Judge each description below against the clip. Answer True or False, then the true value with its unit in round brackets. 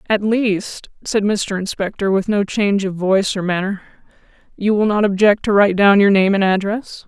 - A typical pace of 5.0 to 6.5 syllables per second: True (5.2 syllables/s)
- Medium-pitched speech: False (200 Hz)